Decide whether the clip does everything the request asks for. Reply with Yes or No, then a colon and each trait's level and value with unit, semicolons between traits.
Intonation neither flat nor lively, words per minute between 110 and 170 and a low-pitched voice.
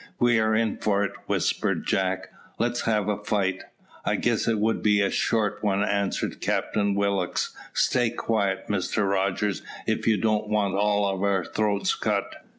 No: narrow, 1.6 semitones; average, 160 wpm; low, 105 Hz